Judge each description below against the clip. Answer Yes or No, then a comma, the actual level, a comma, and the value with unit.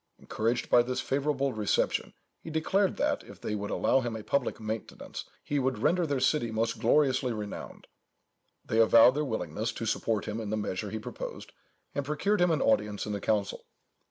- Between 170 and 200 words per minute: Yes, average, 185 wpm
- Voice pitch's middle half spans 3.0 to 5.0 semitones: Yes, average, 4.5 semitones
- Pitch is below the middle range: Yes, low, 115 Hz